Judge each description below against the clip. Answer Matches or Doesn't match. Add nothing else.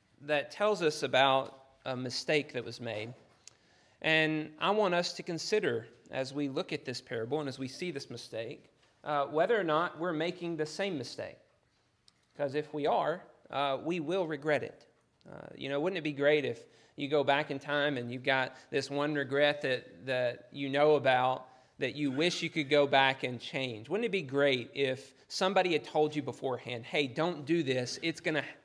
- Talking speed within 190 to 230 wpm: Matches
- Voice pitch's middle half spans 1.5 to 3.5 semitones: Matches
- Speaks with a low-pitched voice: Doesn't match